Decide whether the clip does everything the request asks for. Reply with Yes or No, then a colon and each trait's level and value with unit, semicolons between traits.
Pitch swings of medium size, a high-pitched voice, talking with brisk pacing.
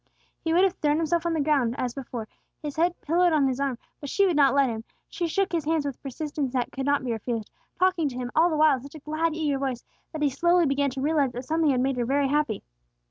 Yes: average, 3.5 semitones; very high, 285 Hz; fast, 270 wpm